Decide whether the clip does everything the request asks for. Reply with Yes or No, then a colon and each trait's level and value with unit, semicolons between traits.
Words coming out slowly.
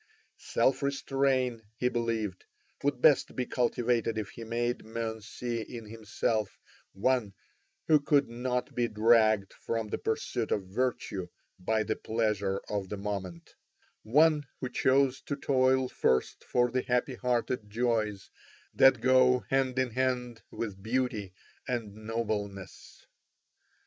Yes: slow, 130 wpm